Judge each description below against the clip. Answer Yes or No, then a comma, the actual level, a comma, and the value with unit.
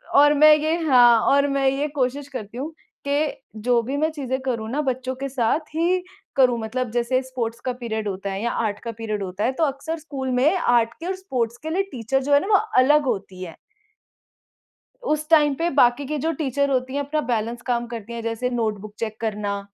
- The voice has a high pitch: Yes, very high, 255 Hz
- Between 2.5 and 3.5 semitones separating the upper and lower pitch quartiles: No, average, 4.1 semitones